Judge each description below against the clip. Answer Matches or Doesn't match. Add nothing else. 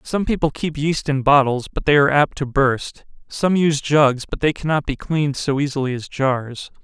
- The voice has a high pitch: Doesn't match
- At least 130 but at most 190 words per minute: Doesn't match